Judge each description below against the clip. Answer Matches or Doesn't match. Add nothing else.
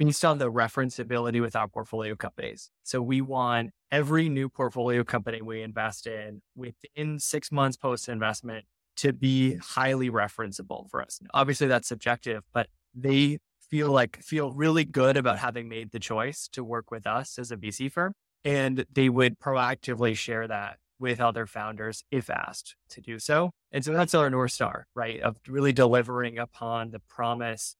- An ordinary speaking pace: Matches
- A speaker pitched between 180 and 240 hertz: Doesn't match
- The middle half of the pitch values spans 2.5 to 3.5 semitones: Matches